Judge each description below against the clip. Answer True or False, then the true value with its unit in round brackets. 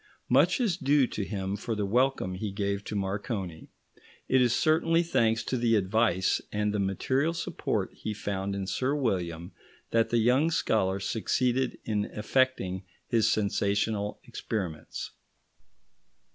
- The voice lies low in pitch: True (105 Hz)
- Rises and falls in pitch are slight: False (4.6 semitones)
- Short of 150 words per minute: True (140 wpm)